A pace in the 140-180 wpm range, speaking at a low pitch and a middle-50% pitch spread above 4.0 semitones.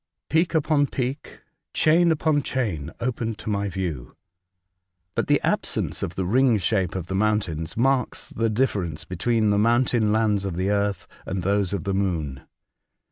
Yes: average, 160 wpm; low, 105 Hz; average, 4.8 semitones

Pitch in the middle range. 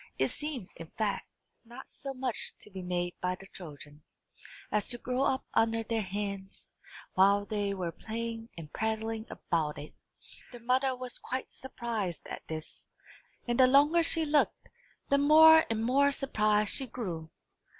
No: high, 225 Hz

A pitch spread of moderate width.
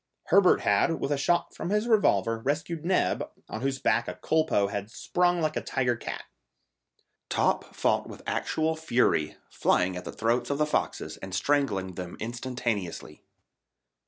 No: wide, 7.1 semitones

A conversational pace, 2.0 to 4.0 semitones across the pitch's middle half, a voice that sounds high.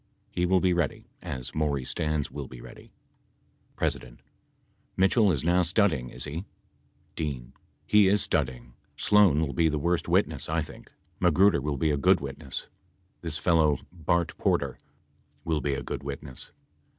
No: average, 155 wpm; average, 3.7 semitones; very low, 80 Hz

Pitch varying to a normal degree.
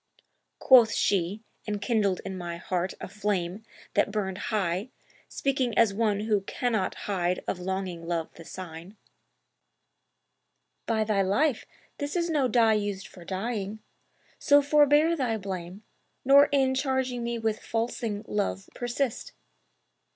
Yes: average, 4.5 semitones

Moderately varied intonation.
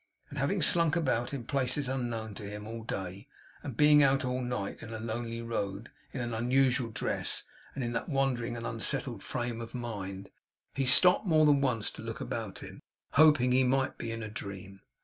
Yes: average, 3.3 semitones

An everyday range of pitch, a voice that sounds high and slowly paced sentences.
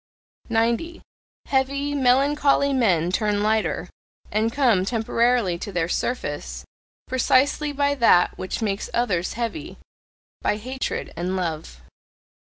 No: wide, 6.2 semitones; high, 230 Hz; slow, 110 wpm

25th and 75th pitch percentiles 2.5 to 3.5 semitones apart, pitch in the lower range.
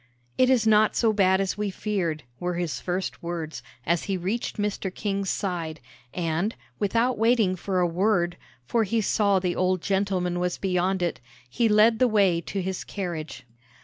No: average, 3.1 semitones; high, 190 Hz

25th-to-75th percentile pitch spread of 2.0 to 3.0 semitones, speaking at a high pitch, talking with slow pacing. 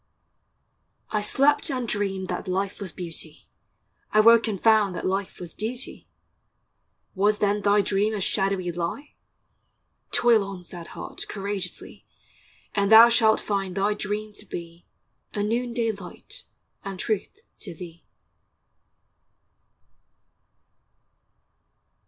Yes: narrow, 2.5 semitones; high, 205 Hz; slow, 115 wpm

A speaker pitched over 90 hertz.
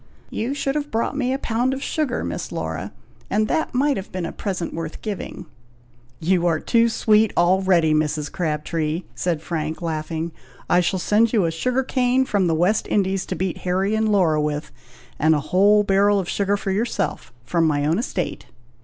Yes: high, 190 Hz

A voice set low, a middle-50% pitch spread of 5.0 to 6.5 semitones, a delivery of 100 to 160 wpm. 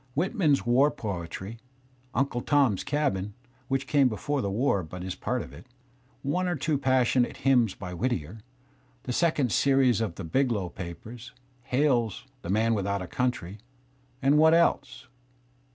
Yes: low, 125 Hz; wide, 5.6 semitones; average, 150 wpm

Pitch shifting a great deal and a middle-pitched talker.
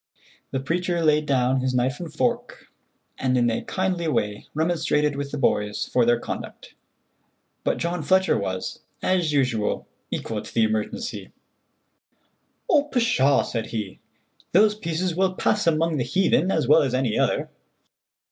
Yes: wide, 6.1 semitones; medium, 150 Hz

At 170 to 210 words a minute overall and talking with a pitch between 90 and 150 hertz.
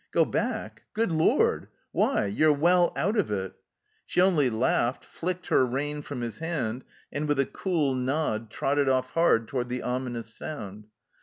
Yes: average, 175 wpm; low, 135 Hz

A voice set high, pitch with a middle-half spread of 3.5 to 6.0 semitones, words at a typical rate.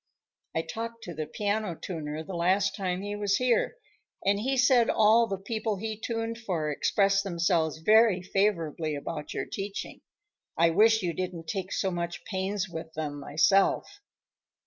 Yes: high, 195 Hz; average, 4.5 semitones; average, 160 wpm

